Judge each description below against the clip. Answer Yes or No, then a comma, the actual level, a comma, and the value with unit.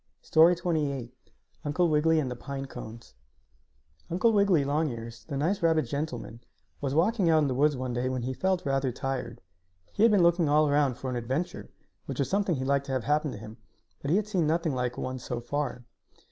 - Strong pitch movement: No, average, 4.3 semitones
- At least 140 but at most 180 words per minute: No, fast, 205 wpm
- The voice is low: No, medium, 145 Hz